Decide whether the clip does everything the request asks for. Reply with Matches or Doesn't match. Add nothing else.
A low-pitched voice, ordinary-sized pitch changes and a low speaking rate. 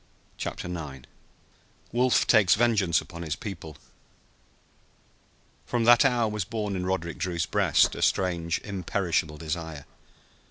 Matches